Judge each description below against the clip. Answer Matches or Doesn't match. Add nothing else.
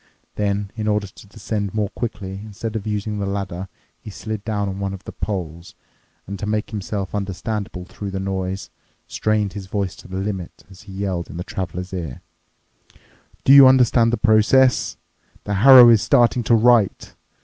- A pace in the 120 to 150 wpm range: Doesn't match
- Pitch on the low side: Matches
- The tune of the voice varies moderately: Doesn't match